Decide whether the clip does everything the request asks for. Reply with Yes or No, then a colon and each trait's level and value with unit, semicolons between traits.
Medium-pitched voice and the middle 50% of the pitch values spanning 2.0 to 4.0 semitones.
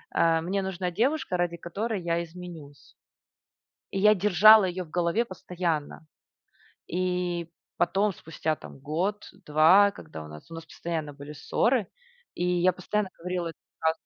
Yes: medium, 175 Hz; average, 2.9 semitones